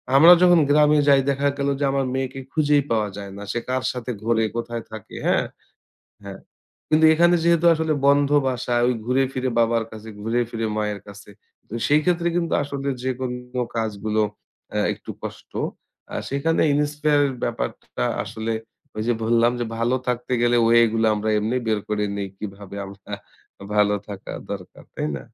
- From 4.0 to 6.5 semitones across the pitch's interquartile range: Yes, average, 4.5 semitones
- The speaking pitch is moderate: No, low, 120 Hz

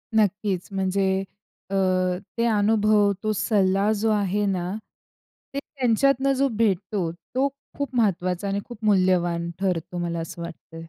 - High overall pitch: Yes, high, 200 Hz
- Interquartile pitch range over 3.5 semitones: No, average, 3.2 semitones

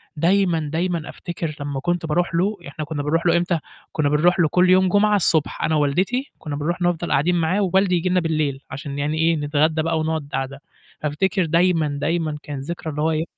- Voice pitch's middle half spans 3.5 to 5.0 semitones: No, average, 2.9 semitones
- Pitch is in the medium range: Yes, medium, 165 Hz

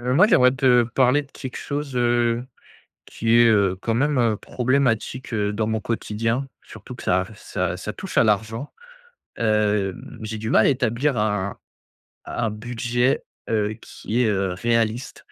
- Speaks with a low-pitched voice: Yes, low, 115 Hz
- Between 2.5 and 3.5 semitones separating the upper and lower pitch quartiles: Yes, average, 2.9 semitones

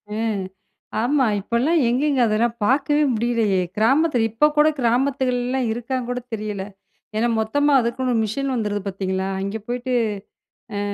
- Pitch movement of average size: Yes, average, 3.4 semitones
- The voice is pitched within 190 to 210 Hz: No, high, 240 Hz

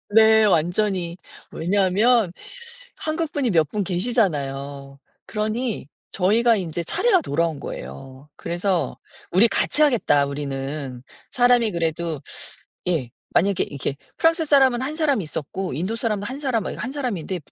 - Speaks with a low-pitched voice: No, high, 190 Hz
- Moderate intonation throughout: No, wide, 7.3 semitones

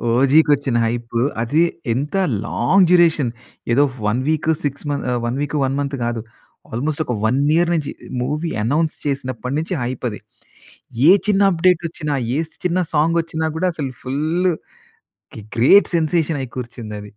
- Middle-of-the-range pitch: Yes, medium, 145 Hz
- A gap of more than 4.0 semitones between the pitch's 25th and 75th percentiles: Yes, average, 4.5 semitones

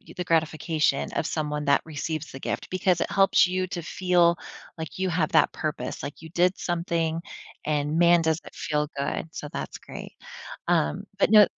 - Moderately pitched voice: Yes, medium, 165 Hz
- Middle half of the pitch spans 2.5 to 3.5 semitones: Yes, average, 2.8 semitones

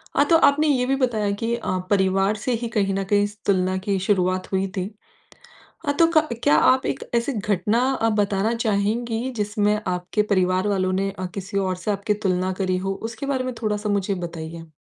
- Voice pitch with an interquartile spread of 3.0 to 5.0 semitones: Yes, average, 3.3 semitones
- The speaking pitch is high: Yes, high, 205 Hz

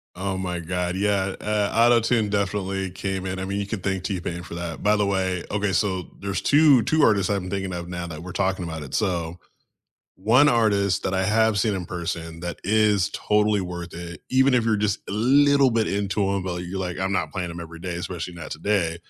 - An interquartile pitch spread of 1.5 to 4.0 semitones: Yes, average, 3.0 semitones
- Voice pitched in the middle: No, very low, 95 Hz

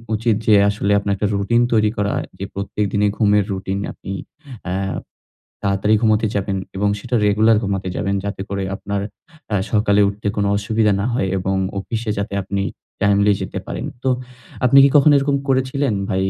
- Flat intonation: Yes, narrow, 1.8 semitones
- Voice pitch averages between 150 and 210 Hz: No, low, 105 Hz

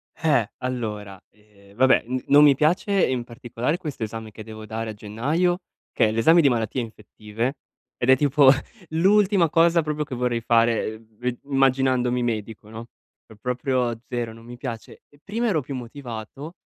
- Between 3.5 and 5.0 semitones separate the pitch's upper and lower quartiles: Yes, average, 4.5 semitones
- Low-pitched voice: Yes, low, 125 Hz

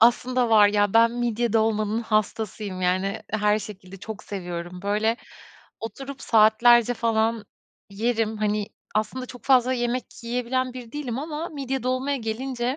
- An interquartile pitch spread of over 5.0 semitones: No, average, 2.9 semitones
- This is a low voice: No, high, 225 Hz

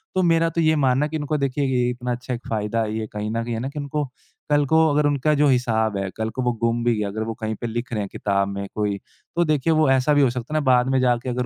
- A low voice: Yes, low, 125 Hz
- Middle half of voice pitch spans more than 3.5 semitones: Yes, average, 4.6 semitones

